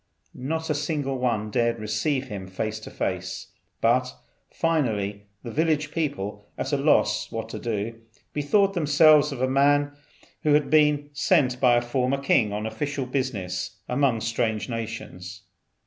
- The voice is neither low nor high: No, low, 125 Hz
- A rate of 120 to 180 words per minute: Yes, average, 150 wpm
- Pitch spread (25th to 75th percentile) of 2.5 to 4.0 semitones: No, average, 5.0 semitones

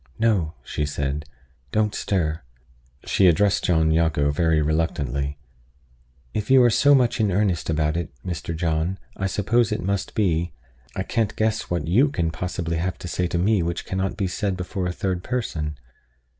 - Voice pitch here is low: Yes, very low, 90 Hz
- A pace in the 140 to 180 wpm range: Yes, average, 170 wpm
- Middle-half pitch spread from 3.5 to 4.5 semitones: Yes, average, 4.2 semitones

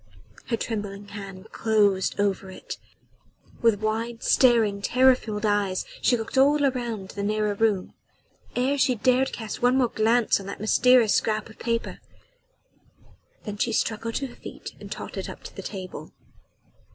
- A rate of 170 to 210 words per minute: No, average, 155 wpm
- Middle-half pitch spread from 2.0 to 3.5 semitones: Yes, average, 2.8 semitones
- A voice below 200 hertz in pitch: No, high, 220 Hz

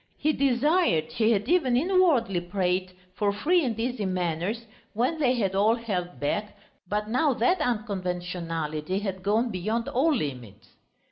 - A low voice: No, high, 210 Hz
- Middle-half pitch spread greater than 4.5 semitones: Yes, wide, 5.6 semitones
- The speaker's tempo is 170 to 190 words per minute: No, average, 145 wpm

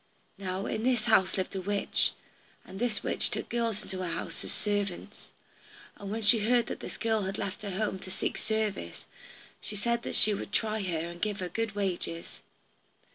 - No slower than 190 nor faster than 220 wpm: Yes, average, 200 wpm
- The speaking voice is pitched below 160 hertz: No, high, 205 Hz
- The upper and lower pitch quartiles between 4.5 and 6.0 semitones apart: No, average, 2.7 semitones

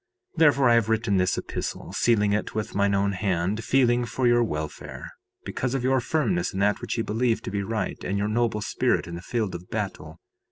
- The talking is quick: Yes, fast, 215 wpm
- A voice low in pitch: Yes, low, 110 Hz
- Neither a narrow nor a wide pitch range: Yes, average, 3.4 semitones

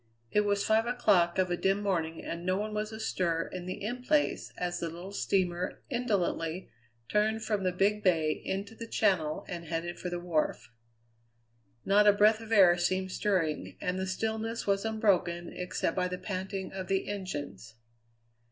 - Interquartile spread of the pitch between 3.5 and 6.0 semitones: No, average, 3.1 semitones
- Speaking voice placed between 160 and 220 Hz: Yes, high, 190 Hz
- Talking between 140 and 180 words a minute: Yes, average, 175 wpm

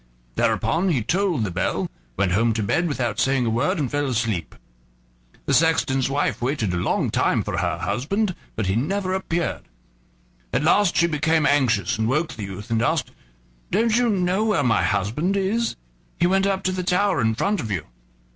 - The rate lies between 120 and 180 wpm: No, average, 190 wpm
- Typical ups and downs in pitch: No, wide, 8.6 semitones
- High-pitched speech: No, medium, 145 Hz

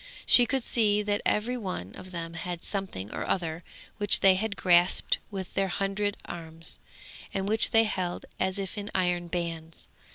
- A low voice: No, high, 190 Hz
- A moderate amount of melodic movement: Yes, average, 3.0 semitones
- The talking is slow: No, average, 170 wpm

